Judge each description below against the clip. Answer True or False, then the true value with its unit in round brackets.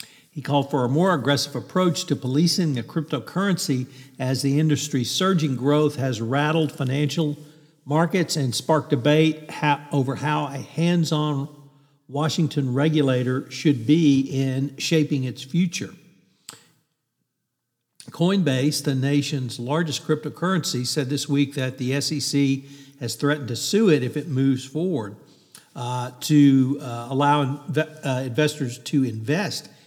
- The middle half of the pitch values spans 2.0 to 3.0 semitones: True (2.5 semitones)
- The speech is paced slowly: True (130 wpm)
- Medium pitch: True (145 Hz)